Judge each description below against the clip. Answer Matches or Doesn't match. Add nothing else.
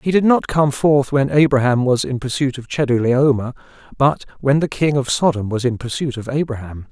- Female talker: Doesn't match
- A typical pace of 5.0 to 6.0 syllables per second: Matches